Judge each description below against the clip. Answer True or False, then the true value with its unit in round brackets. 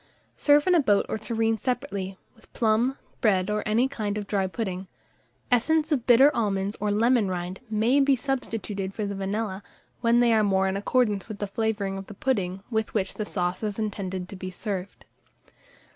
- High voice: True (210 Hz)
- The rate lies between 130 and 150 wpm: False (190 wpm)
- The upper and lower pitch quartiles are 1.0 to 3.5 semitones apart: True (3.2 semitones)